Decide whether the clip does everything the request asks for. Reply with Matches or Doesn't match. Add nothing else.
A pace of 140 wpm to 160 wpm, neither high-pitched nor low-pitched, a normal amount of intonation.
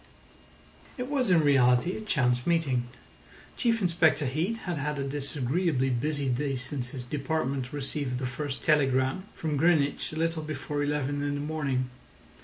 Matches